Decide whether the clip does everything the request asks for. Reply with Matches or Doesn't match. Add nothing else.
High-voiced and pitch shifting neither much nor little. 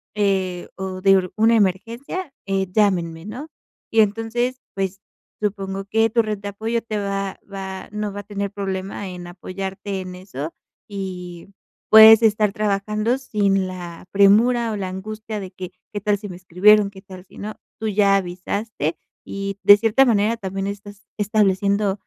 Doesn't match